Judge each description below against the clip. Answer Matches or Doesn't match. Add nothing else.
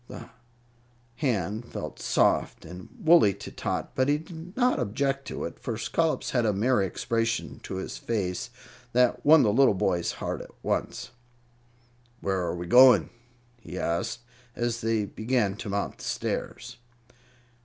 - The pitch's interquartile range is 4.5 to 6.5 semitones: Matches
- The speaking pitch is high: Doesn't match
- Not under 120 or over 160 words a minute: Matches